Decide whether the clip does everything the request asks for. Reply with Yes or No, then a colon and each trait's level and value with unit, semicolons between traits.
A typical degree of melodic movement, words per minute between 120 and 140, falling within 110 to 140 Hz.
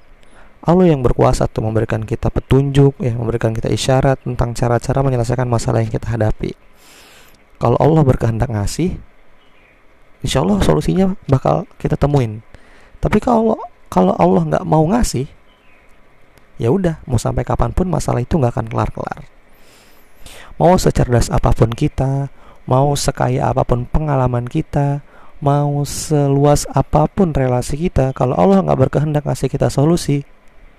Yes: average, 3.7 semitones; average, 130 wpm; low, 135 Hz